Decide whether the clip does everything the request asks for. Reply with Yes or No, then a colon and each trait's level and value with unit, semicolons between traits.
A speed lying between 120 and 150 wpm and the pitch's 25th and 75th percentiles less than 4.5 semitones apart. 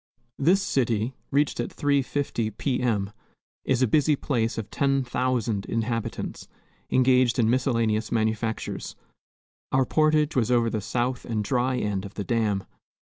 Yes: average, 145 wpm; average, 3.1 semitones